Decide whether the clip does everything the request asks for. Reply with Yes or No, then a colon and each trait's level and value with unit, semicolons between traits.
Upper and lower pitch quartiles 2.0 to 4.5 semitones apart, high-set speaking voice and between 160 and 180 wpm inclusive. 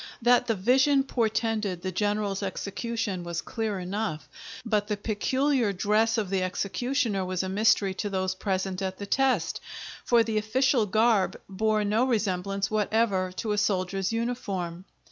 No: average, 3.1 semitones; high, 210 Hz; average, 150 wpm